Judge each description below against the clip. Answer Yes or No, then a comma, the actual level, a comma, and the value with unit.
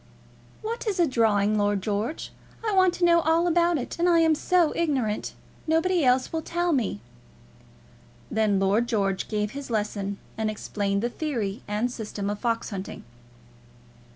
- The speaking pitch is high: Yes, high, 240 Hz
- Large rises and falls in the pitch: Yes, wide, 8.0 semitones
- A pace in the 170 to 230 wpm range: No, average, 155 wpm